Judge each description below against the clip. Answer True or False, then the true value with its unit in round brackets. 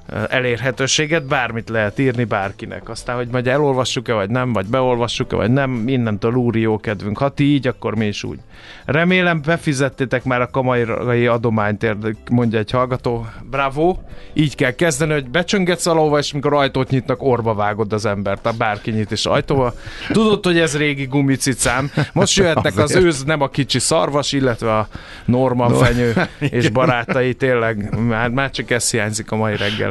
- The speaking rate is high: True (165 wpm)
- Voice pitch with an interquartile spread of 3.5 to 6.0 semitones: True (3.8 semitones)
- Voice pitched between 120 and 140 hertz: True (125 Hz)